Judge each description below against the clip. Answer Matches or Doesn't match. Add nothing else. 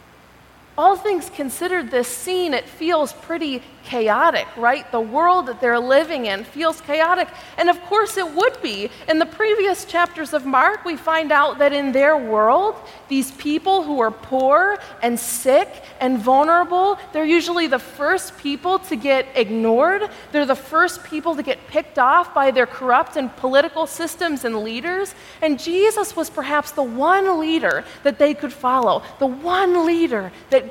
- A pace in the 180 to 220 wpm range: Doesn't match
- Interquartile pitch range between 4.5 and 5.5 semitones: Matches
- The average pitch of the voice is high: Matches